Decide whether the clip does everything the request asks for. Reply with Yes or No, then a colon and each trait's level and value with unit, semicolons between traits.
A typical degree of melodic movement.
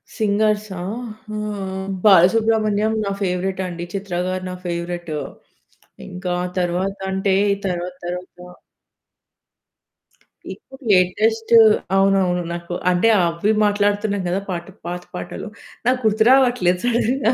Yes: average, 3.1 semitones